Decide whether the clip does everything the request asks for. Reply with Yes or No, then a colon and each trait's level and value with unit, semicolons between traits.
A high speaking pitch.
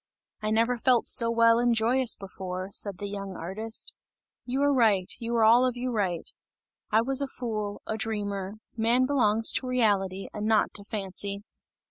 Yes: high, 220 Hz